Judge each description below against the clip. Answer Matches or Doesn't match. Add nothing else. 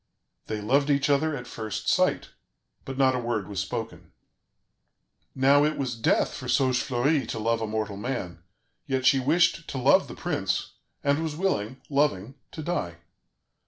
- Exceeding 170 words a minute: Doesn't match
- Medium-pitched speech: Doesn't match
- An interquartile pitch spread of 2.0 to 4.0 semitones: Doesn't match